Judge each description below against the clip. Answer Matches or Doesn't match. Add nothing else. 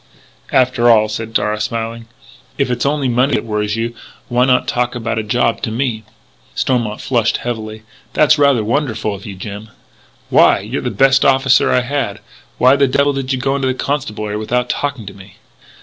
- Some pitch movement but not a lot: Matches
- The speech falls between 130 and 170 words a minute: Doesn't match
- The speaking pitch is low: Matches